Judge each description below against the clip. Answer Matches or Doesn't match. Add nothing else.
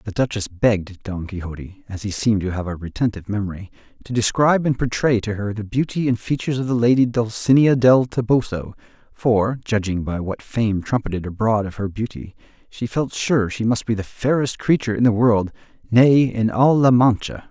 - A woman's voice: Doesn't match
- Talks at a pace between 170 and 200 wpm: Matches